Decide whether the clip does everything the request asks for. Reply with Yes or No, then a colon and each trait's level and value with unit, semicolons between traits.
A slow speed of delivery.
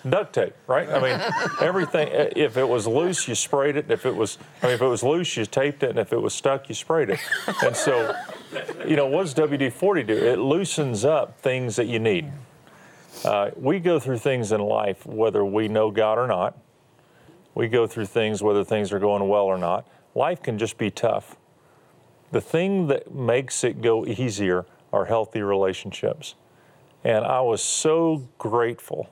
No: average, 190 wpm